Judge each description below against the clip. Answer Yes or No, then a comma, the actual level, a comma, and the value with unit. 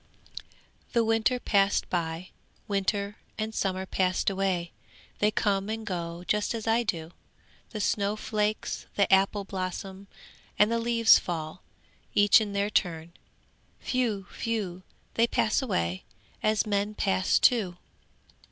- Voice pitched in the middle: No, high, 200 Hz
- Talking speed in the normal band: No, slow, 130 wpm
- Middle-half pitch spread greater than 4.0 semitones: No, average, 2.8 semitones